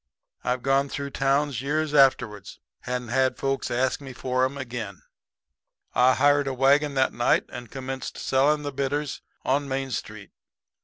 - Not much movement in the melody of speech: Yes, narrow, 1.9 semitones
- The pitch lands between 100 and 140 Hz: Yes, low, 135 Hz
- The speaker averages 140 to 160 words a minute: Yes, average, 150 wpm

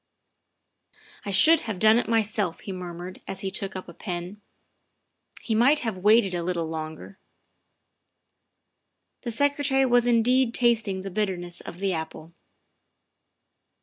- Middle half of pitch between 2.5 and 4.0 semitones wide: No, average, 4.7 semitones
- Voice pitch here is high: Yes, high, 200 Hz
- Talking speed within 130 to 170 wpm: Yes, average, 150 wpm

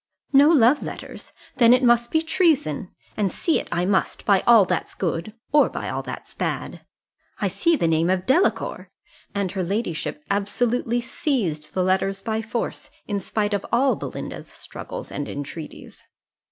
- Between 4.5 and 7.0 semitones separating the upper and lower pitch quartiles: Yes, average, 5.0 semitones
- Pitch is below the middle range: No, high, 210 Hz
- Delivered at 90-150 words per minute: No, average, 165 wpm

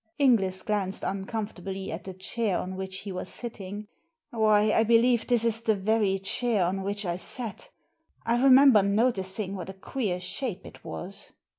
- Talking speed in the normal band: Yes, average, 165 wpm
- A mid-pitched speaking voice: No, high, 205 Hz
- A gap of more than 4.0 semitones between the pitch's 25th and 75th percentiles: No, average, 3.3 semitones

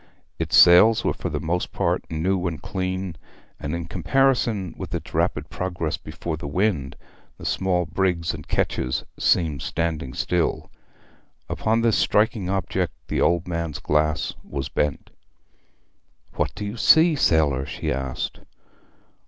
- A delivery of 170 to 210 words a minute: No, average, 140 wpm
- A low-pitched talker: Yes, very low, 85 Hz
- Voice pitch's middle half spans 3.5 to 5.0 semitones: Yes, average, 3.9 semitones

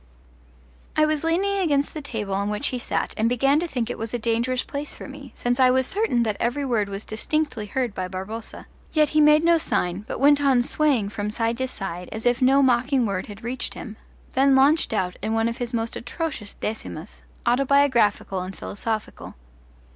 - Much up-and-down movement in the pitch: No, average, 4.5 semitones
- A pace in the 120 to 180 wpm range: No, average, 200 wpm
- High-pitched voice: Yes, high, 245 Hz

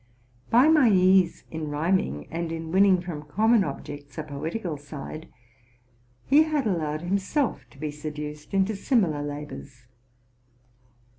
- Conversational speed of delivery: No, slow, 130 wpm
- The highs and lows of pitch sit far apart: No, average, 4.8 semitones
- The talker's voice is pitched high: No, medium, 165 Hz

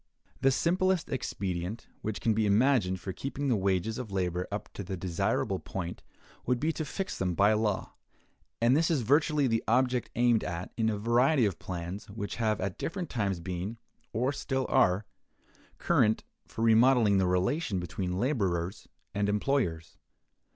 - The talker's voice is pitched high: No, low, 110 Hz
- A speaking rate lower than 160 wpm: No, average, 165 wpm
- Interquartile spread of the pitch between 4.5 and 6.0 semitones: Yes, wide, 5.4 semitones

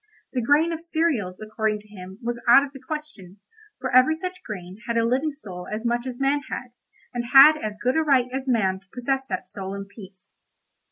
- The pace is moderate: No, fast, 215 wpm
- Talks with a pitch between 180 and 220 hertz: No, high, 240 Hz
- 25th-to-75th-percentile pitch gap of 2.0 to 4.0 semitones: No, wide, 5.4 semitones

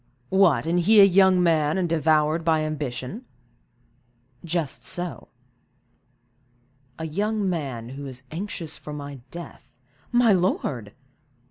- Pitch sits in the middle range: Yes, medium, 165 Hz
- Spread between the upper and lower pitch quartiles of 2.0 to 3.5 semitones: No, average, 4.0 semitones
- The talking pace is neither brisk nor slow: No, slow, 120 wpm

